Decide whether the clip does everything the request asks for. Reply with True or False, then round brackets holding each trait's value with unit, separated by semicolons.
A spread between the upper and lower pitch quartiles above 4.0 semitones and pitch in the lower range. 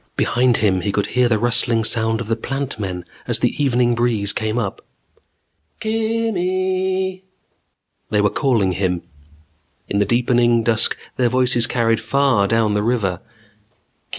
False (3.4 semitones; 120 Hz)